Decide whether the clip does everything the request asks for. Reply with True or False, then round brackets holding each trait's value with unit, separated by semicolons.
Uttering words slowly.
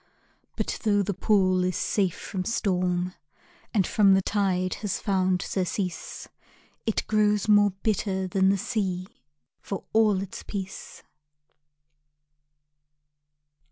True (115 wpm)